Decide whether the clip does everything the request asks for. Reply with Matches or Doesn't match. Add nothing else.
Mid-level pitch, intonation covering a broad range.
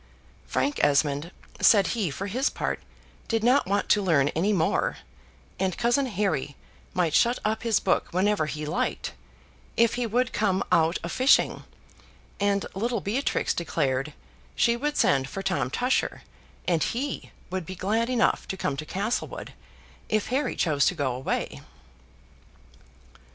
Doesn't match